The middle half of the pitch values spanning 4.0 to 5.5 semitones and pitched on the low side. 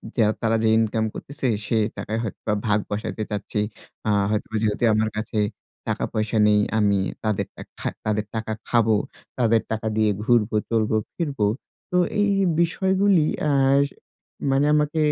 Yes: average, 4.3 semitones; low, 110 Hz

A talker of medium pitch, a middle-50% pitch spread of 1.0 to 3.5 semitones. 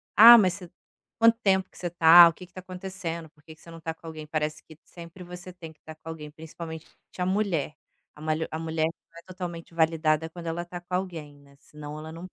Yes: medium, 165 Hz; narrow, 2.4 semitones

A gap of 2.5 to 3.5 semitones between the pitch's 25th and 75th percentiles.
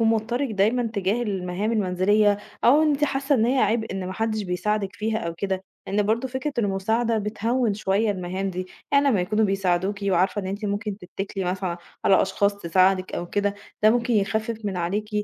Yes: average, 2.8 semitones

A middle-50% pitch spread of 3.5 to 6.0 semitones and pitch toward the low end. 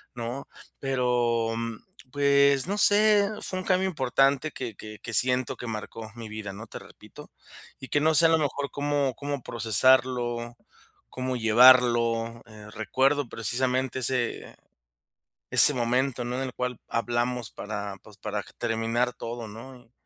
No: average, 2.8 semitones; low, 125 Hz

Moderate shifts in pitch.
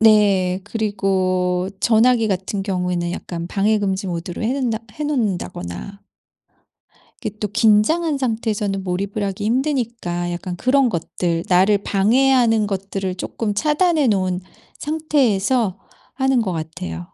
Yes: average, 4.3 semitones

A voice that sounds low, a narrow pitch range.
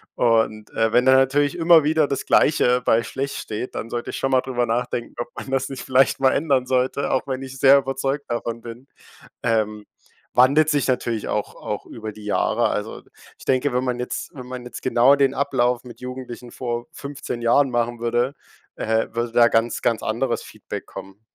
Yes: low, 125 Hz; narrow, 2.3 semitones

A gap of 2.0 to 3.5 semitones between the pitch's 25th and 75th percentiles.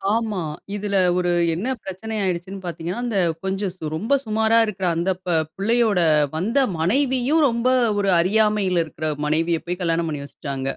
No: average, 4.4 semitones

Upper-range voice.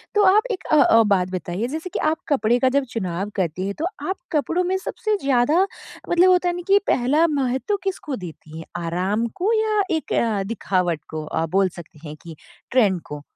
Yes: high, 245 Hz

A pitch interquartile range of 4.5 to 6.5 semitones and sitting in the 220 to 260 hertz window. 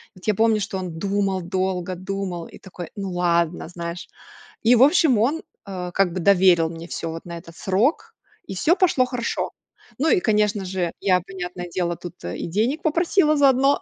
No: average, 5.2 semitones; high, 190 Hz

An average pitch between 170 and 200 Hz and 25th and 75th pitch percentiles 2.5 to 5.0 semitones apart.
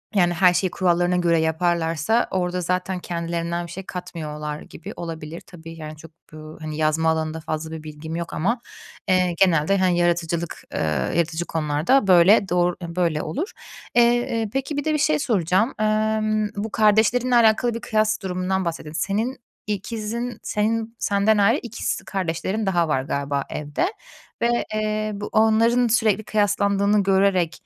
Yes: medium, 185 Hz; average, 4.6 semitones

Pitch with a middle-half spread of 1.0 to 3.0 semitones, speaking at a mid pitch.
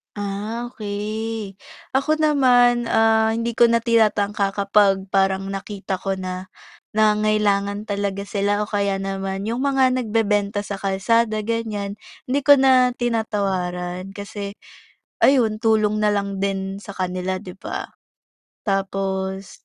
No: narrow, 2.5 semitones; high, 205 Hz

